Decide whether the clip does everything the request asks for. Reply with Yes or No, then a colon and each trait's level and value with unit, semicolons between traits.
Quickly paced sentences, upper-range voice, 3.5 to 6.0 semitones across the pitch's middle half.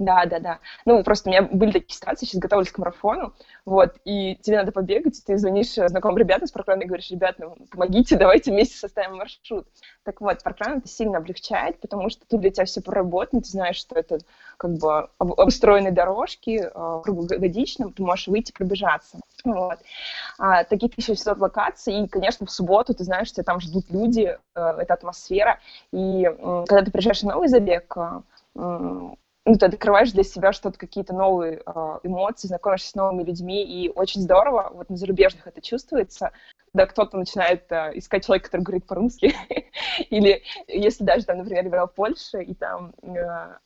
No: fast, 175 wpm; high, 195 Hz; average, 2.7 semitones